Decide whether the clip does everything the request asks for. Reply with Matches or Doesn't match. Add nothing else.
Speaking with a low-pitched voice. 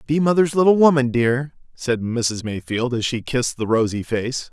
Matches